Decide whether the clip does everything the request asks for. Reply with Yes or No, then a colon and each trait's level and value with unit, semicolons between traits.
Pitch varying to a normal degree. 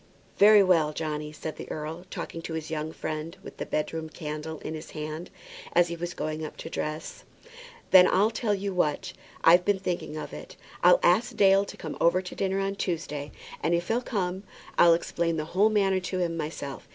Yes: average, 3.5 semitones